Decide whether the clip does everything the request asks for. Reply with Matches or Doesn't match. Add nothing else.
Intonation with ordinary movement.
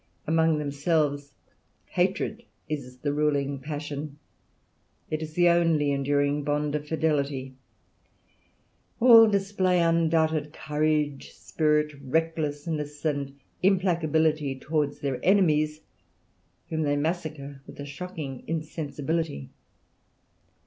Doesn't match